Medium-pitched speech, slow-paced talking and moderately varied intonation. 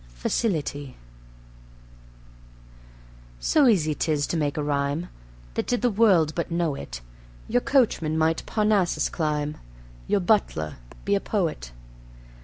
No: medium, 160 Hz; slow, 120 wpm; wide, 5.7 semitones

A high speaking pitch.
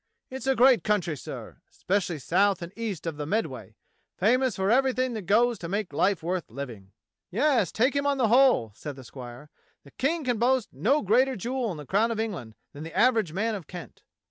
Yes: high, 210 Hz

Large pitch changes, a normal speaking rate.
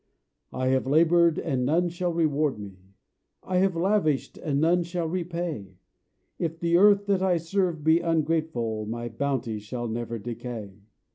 Yes: wide, 6.3 semitones; average, 150 wpm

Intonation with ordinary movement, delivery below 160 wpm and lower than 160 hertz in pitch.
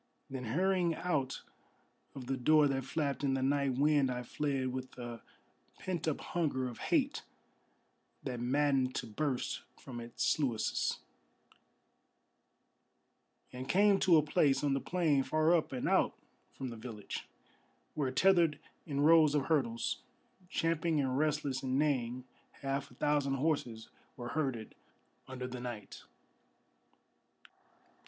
Yes: average, 3.3 semitones; slow, 135 wpm; low, 135 Hz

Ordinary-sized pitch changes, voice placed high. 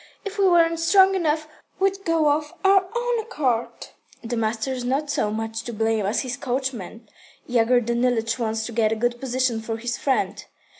No: wide, 6.6 semitones; very high, 250 Hz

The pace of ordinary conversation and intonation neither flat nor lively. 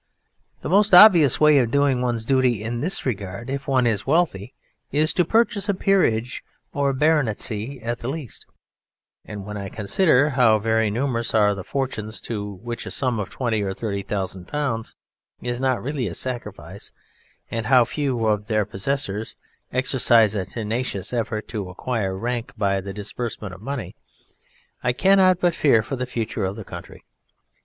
Yes: average, 170 wpm; average, 4.6 semitones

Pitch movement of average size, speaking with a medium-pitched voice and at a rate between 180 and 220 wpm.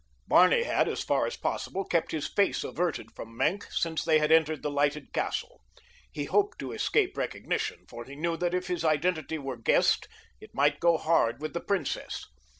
Yes: average, 3.6 semitones; medium, 160 Hz; average, 190 wpm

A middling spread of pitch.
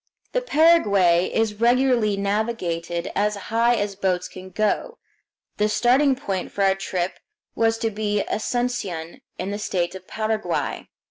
Yes: average, 3.7 semitones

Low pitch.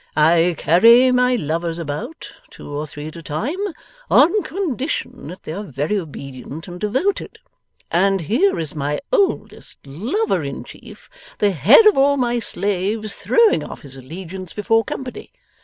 No: high, 195 Hz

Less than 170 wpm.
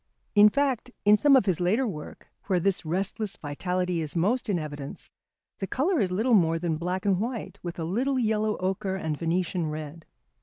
No: average, 190 wpm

